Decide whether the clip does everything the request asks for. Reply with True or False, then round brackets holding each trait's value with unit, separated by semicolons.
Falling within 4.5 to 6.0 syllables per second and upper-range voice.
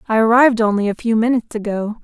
False (7.2 syllables/s; 225 Hz)